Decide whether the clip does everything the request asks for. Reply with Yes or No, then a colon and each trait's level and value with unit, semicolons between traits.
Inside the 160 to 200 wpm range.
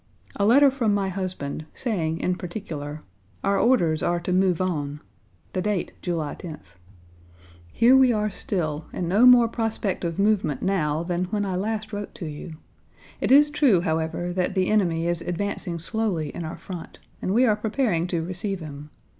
Yes: average, 175 wpm